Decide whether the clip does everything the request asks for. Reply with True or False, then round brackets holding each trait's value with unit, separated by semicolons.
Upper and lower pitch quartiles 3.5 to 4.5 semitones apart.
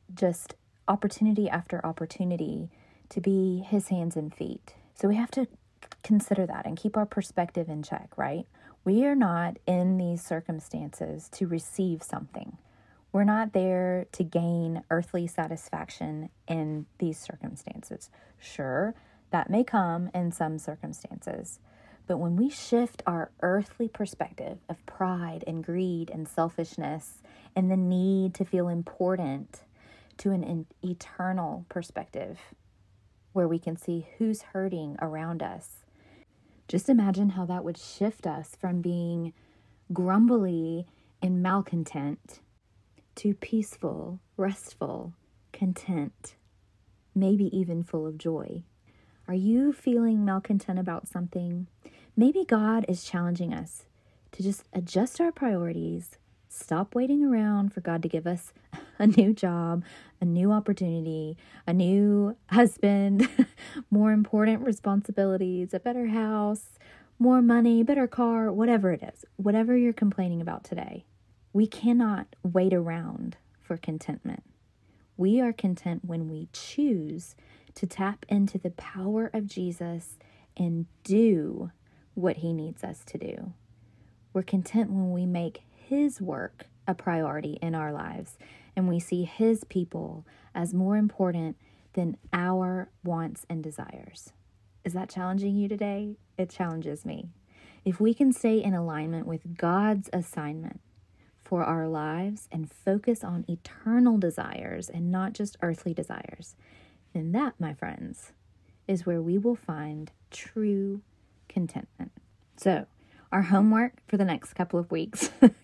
True (4.0 semitones)